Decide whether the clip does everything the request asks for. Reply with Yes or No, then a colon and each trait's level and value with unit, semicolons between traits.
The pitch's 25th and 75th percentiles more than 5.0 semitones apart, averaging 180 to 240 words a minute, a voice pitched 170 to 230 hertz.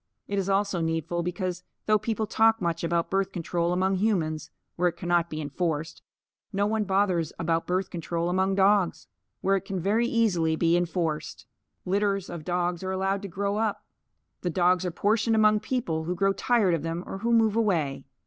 No: average, 3.1 semitones; average, 185 wpm; medium, 185 Hz